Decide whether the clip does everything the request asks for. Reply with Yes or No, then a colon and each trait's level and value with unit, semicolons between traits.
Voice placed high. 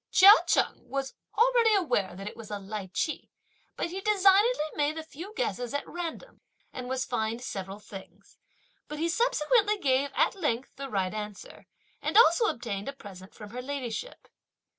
Yes: very high, 275 Hz